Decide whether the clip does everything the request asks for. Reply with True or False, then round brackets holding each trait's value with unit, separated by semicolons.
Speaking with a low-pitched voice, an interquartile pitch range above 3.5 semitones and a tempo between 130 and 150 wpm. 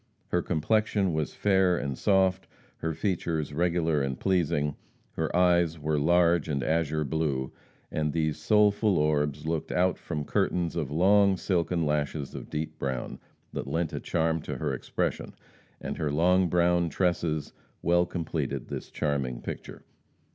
False (80 Hz; 2.9 semitones; 145 wpm)